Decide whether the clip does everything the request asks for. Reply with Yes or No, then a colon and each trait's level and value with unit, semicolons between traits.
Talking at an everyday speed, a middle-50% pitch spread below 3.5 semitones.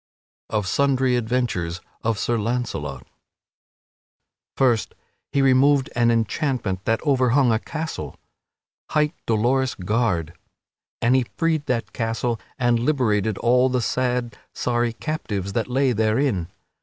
No: slow, 120 wpm; average, 3.0 semitones